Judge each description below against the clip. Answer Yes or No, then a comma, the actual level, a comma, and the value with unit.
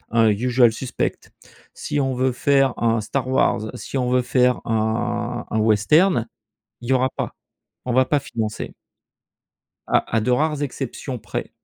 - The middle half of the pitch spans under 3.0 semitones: Yes, narrow, 2.5 semitones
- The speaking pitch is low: Yes, low, 125 Hz